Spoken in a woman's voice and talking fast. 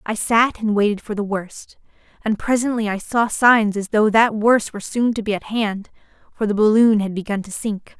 Yes: female; fast, 220 wpm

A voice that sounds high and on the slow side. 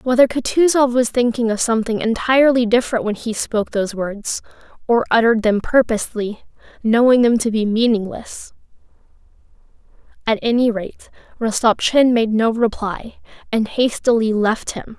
Yes: high, 230 Hz; slow, 130 wpm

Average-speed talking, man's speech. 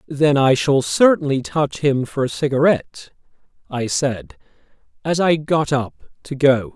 Yes: average, 150 wpm; male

